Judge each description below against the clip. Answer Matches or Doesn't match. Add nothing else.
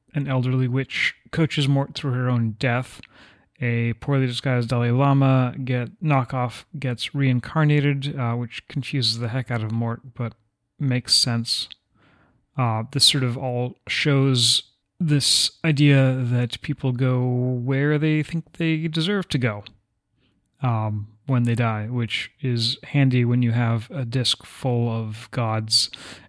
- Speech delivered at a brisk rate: Doesn't match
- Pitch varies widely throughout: Doesn't match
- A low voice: Matches